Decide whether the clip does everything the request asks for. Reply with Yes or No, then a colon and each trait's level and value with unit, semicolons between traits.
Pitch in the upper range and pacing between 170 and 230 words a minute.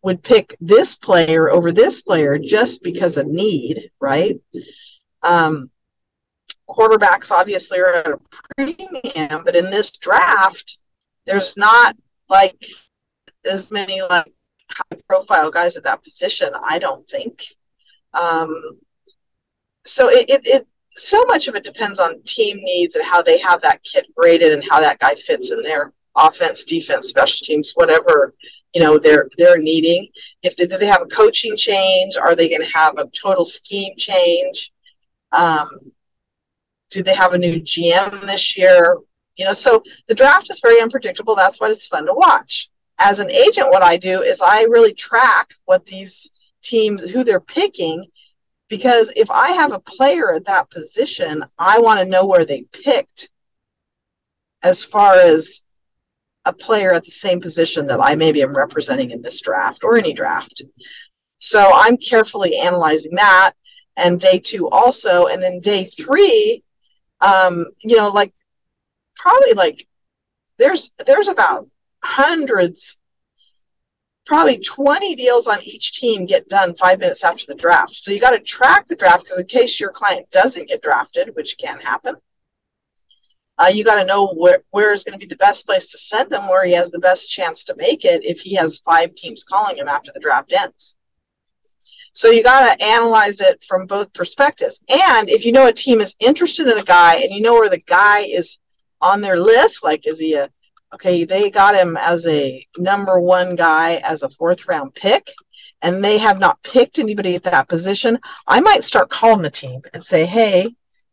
Yes: high, 215 Hz; average, 175 wpm